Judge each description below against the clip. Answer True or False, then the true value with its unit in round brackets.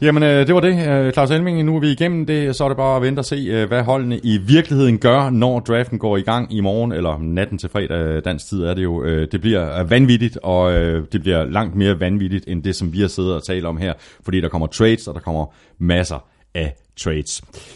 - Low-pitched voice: True (100 Hz)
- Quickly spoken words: True (235 wpm)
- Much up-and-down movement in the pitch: True (6.9 semitones)